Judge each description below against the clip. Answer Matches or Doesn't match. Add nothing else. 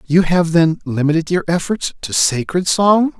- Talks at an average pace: Matches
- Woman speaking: Doesn't match